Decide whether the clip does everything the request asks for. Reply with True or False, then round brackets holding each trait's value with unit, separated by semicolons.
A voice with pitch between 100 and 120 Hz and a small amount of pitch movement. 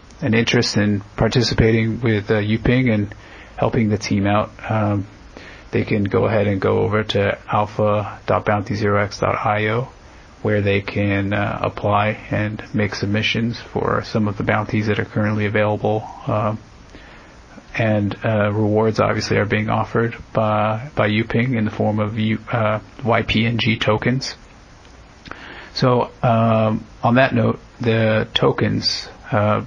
True (110 Hz; 1.5 semitones)